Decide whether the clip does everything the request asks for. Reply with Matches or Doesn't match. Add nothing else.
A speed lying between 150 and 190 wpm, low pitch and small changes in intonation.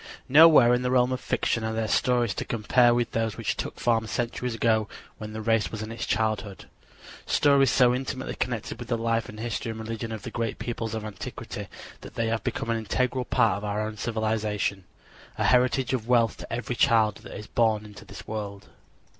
Doesn't match